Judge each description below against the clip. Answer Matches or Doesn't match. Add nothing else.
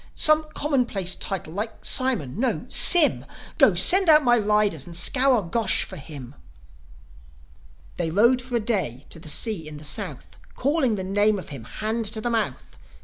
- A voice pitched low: Doesn't match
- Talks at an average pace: Matches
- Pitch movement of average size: Doesn't match